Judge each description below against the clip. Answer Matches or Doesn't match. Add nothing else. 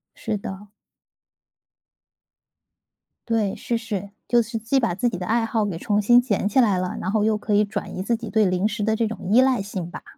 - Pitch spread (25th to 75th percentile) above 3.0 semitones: Doesn't match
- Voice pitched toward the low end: Doesn't match